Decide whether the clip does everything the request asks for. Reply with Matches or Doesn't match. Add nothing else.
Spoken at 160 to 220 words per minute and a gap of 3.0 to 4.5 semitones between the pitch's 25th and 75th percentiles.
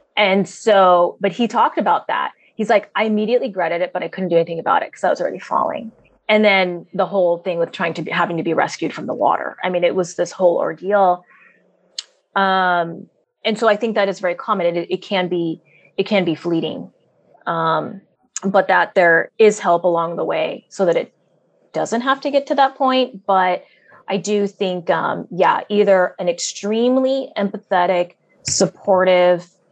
Matches